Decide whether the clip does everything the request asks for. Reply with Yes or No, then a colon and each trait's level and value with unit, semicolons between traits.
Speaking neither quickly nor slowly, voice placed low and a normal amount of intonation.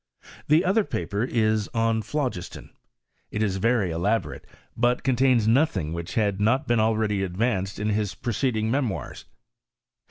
No: slow, 125 wpm; low, 110 Hz; average, 3.6 semitones